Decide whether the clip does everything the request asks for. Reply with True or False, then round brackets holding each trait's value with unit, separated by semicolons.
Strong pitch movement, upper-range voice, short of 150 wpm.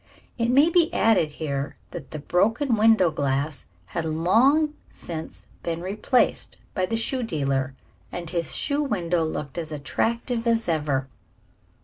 False (7.2 semitones; 175 Hz; 140 wpm)